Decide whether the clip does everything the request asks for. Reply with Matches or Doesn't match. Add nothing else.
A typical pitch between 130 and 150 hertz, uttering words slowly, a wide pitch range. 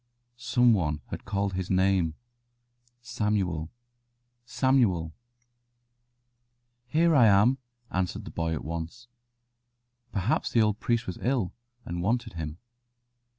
Doesn't match